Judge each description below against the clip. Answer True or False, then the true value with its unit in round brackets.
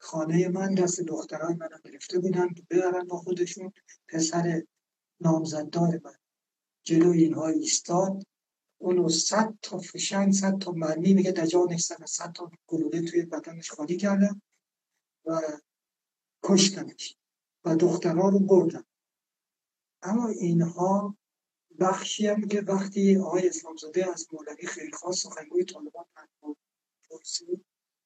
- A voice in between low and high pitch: True (175 Hz)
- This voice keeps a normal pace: True (115 wpm)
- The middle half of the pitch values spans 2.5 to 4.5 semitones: True (2.9 semitones)